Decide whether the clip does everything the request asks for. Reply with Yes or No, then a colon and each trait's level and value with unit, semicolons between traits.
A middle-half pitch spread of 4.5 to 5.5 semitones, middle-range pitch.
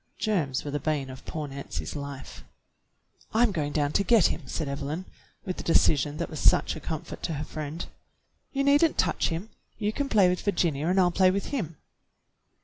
Yes: average, 5.2 semitones; medium, 160 Hz